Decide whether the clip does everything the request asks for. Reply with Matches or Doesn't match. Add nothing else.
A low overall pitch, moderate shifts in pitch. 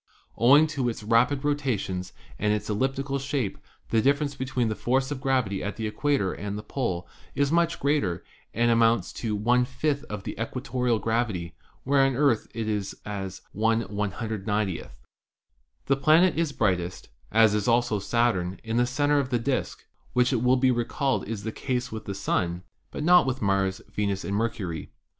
Matches